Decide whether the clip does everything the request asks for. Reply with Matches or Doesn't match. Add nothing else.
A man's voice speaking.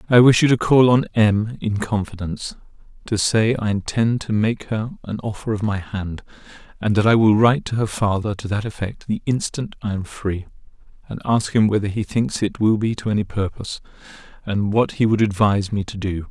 Matches